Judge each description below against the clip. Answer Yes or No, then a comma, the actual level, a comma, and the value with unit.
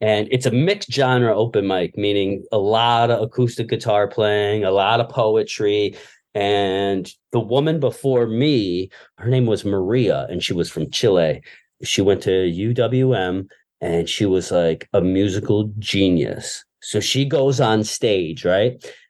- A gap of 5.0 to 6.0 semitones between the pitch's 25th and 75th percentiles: No, average, 4.4 semitones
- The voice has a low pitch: Yes, low, 110 Hz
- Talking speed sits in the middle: Yes, average, 155 wpm